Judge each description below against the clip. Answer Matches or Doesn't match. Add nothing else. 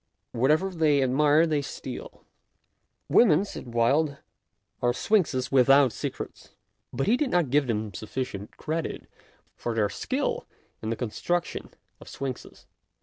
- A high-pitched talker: Doesn't match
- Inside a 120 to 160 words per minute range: Matches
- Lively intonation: Doesn't match